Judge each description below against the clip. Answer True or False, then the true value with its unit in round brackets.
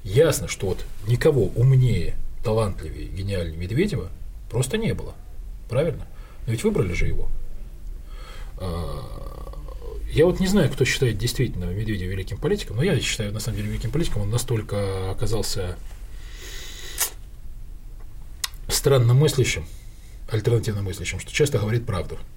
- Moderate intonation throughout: True (5.0 semitones)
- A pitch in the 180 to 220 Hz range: False (105 Hz)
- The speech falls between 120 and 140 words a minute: True (125 wpm)